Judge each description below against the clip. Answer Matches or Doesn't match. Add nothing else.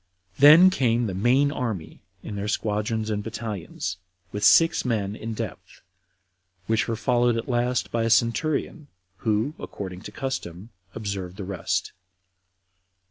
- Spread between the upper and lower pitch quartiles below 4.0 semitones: Matches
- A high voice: Doesn't match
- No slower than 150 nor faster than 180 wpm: Doesn't match